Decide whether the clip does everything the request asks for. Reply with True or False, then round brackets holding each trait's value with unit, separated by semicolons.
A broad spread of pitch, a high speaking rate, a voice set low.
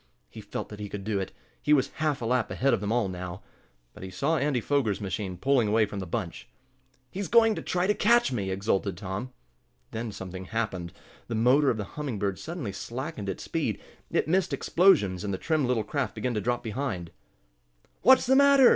True (6.7 semitones; 210 wpm; 115 Hz)